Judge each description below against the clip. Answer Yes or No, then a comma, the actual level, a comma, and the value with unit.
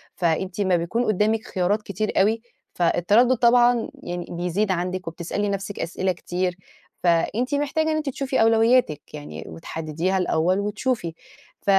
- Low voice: No, high, 195 Hz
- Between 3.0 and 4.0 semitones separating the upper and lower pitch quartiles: No, average, 4.5 semitones